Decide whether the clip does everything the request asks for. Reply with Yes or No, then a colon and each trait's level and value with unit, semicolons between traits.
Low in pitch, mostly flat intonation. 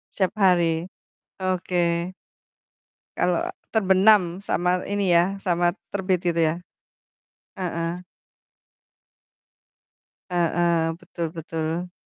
No: medium, 175 Hz; narrow, 1.7 semitones